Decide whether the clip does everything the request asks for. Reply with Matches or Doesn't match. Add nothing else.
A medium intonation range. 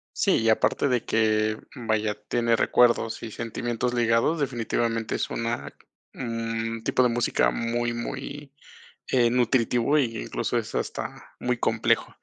Doesn't match